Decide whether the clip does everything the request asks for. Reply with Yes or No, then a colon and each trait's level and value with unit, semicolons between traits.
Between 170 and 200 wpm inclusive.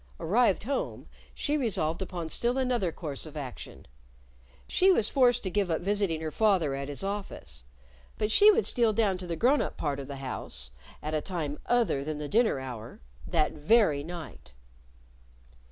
Yes: average, 175 wpm